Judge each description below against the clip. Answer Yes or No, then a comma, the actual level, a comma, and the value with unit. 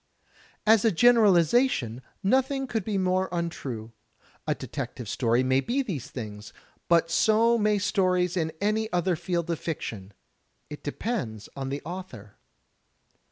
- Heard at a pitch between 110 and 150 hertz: No, medium, 180 Hz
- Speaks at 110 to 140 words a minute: Yes, slow, 135 wpm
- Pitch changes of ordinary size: No, wide, 8.1 semitones